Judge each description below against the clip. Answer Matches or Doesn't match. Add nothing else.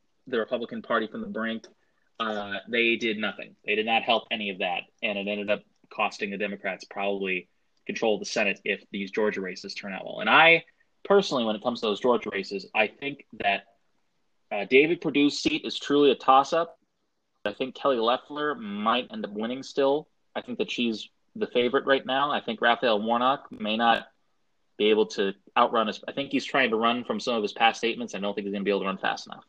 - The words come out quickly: Matches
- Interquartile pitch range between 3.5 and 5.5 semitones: Matches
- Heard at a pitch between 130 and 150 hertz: Doesn't match